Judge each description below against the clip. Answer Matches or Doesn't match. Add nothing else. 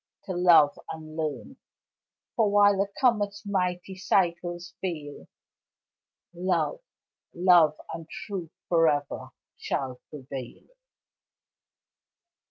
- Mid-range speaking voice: Matches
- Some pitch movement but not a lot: Matches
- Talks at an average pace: Doesn't match